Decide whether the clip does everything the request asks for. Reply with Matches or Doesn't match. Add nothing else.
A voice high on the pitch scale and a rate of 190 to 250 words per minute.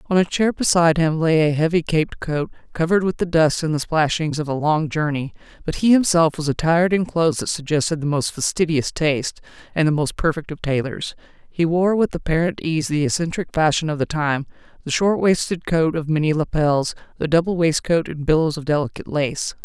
Doesn't match